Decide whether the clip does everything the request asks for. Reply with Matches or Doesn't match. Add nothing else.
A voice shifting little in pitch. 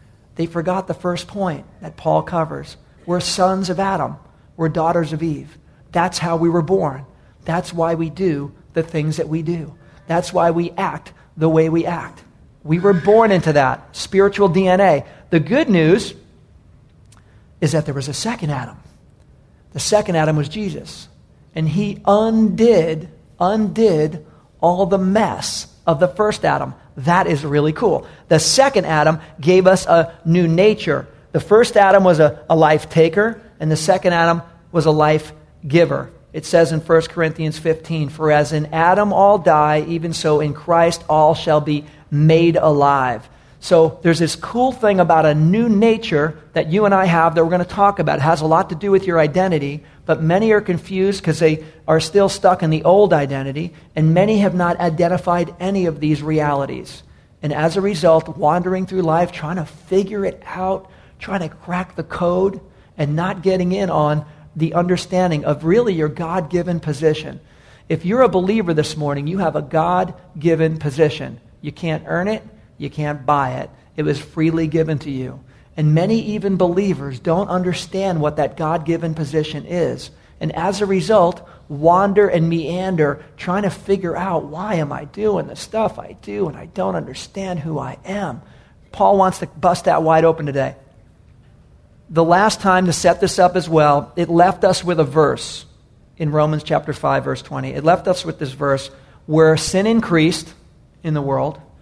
Doesn't match